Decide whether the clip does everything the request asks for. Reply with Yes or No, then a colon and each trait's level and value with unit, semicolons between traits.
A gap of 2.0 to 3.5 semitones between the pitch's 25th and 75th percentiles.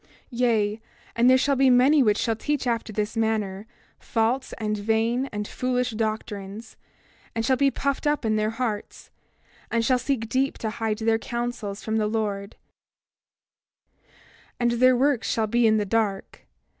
Yes: narrow, 2.6 semitones